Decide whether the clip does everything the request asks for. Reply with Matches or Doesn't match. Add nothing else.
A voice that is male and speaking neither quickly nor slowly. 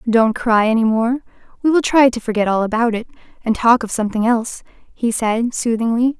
Doesn't match